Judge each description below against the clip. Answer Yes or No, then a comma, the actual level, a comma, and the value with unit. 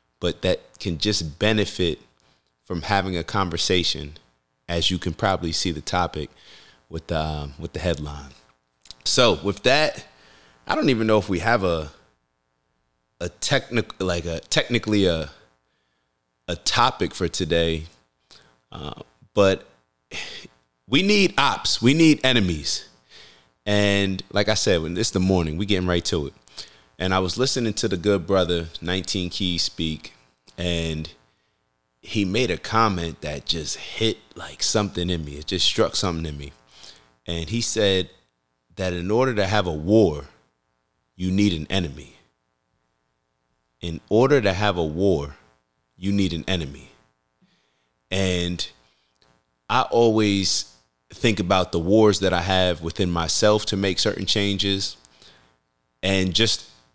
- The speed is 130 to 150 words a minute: Yes, average, 140 wpm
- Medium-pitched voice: No, very low, 85 Hz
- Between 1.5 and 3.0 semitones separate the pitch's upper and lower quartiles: No, wide, 8.2 semitones